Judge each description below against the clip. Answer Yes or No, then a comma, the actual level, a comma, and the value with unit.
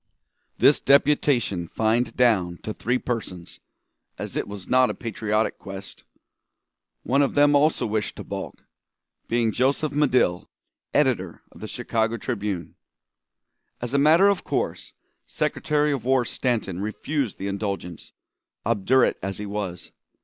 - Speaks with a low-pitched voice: Yes, low, 115 Hz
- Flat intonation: No, average, 5.1 semitones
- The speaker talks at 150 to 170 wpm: No, slow, 135 wpm